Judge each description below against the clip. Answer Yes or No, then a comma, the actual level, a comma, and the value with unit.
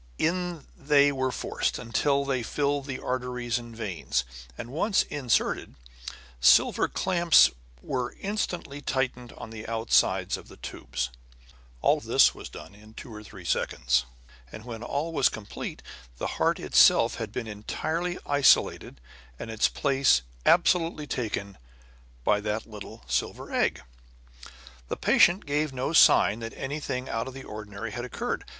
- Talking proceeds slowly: No, average, 145 wpm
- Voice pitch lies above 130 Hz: No, low, 125 Hz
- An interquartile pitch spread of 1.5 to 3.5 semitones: No, average, 4.7 semitones